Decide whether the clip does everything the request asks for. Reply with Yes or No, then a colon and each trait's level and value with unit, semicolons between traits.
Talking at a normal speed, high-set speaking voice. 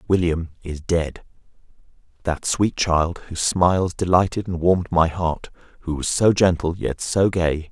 No: average, 150 wpm; very low, 85 Hz